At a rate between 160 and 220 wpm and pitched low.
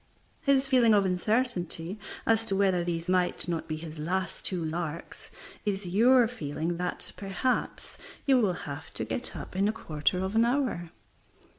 No: average, 165 wpm; high, 190 Hz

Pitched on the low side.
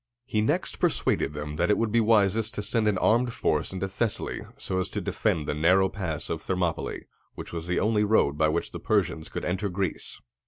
Yes: very low, 95 Hz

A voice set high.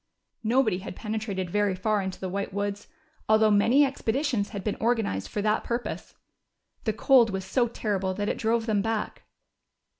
Yes: high, 215 Hz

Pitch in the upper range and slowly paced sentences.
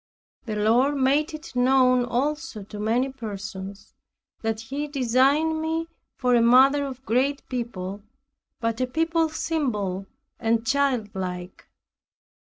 Yes: very high, 250 Hz; slow, 120 wpm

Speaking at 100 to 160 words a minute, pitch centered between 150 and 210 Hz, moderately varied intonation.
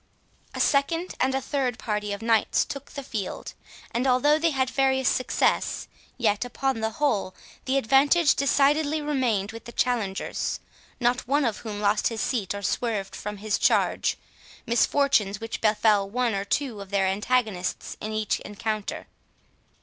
No: average, 155 wpm; high, 235 Hz; average, 4.5 semitones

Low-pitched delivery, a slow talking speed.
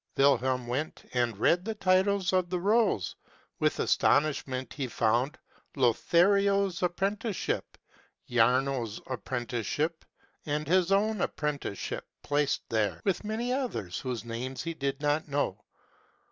No: medium, 145 Hz; slow, 120 wpm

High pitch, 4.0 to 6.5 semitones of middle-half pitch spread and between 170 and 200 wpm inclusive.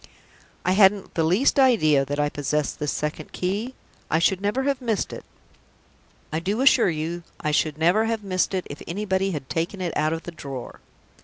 No: medium, 180 Hz; average, 5.0 semitones; average, 190 wpm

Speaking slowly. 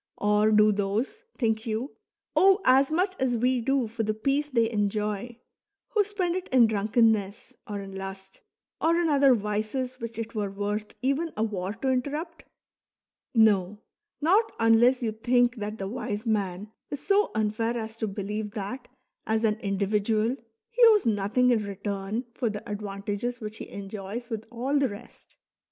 No: average, 165 wpm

